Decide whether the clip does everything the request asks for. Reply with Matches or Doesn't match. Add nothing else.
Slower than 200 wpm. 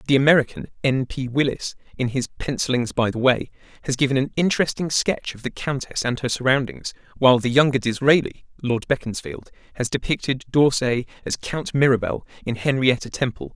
Matches